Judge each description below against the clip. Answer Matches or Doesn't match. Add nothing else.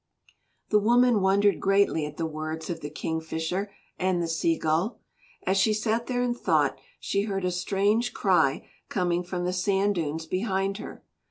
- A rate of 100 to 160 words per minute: Doesn't match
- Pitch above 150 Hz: Matches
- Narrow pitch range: Doesn't match